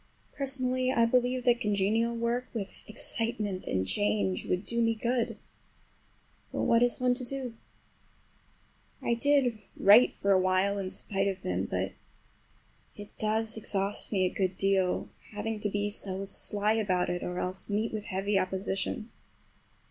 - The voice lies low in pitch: No, high, 210 Hz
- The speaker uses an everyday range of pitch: Yes, average, 3.6 semitones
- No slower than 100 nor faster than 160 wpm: Yes, average, 150 wpm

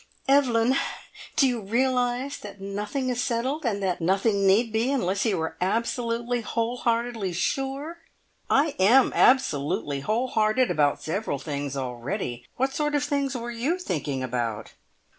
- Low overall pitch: No, high, 230 Hz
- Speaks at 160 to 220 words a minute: No, average, 145 wpm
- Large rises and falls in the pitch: Yes, wide, 5.8 semitones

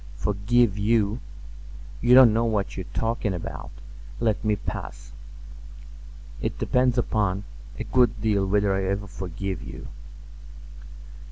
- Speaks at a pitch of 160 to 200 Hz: No, low, 105 Hz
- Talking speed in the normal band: No, slow, 120 wpm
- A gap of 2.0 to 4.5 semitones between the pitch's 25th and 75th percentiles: Yes, average, 3.0 semitones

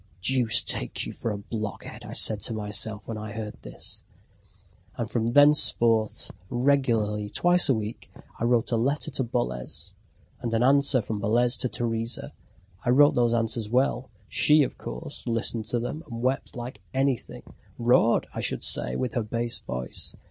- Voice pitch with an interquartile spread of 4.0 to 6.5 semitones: No, average, 2.7 semitones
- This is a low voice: Yes, low, 115 Hz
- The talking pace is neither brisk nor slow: Yes, average, 170 wpm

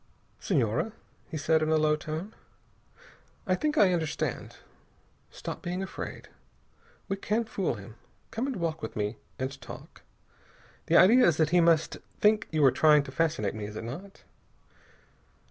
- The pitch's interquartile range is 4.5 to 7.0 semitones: Yes, average, 5.3 semitones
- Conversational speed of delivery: Yes, average, 160 wpm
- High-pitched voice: No, medium, 160 Hz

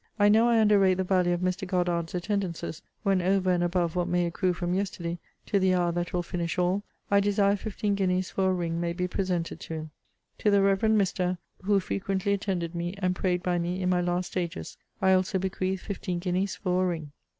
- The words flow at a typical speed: No, fast, 215 wpm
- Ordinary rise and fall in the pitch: No, narrow, 1.8 semitones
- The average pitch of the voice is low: No, medium, 185 Hz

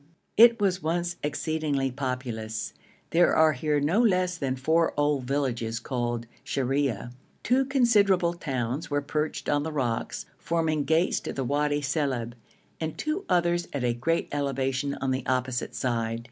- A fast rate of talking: No, average, 150 wpm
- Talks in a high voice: No, medium, 145 Hz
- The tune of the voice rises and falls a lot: No, average, 4.5 semitones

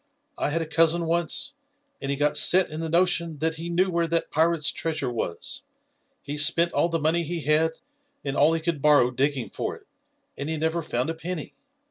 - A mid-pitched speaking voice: Yes, medium, 160 Hz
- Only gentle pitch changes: Yes, narrow, 2.2 semitones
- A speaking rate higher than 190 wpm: Yes, fast, 205 wpm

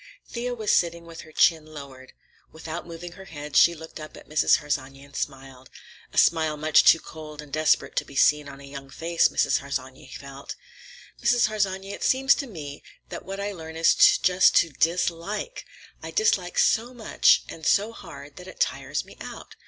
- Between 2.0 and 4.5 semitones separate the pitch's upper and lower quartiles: No, average, 4.9 semitones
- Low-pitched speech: No, medium, 160 Hz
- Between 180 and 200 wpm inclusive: Yes, average, 190 wpm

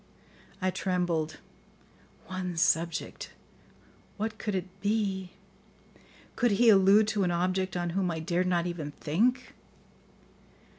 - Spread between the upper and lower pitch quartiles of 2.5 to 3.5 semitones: Yes, average, 2.8 semitones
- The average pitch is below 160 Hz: No, medium, 185 Hz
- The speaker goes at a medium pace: No, slow, 115 wpm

